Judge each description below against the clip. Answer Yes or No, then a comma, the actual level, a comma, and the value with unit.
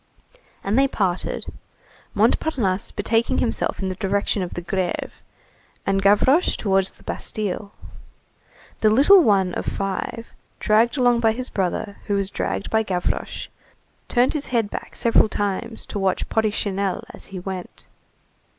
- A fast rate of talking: No, average, 140 wpm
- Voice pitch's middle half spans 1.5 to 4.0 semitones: Yes, average, 3.1 semitones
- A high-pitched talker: Yes, high, 205 Hz